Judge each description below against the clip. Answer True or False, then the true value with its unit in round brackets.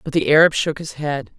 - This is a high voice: False (150 Hz)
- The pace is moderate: False (260 wpm)